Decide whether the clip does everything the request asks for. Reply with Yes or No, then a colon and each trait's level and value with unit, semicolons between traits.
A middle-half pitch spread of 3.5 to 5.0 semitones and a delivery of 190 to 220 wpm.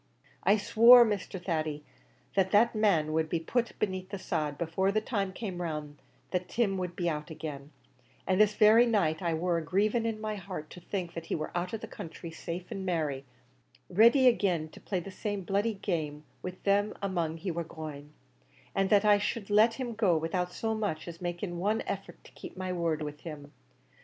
Yes: average, 4.2 semitones; average, 200 wpm